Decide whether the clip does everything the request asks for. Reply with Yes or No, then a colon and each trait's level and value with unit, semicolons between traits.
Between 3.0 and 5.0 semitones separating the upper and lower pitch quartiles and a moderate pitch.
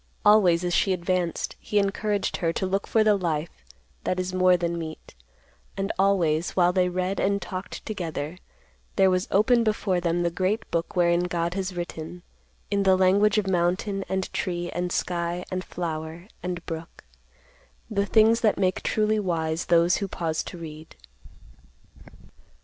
No: narrow, 2.4 semitones; medium, 180 Hz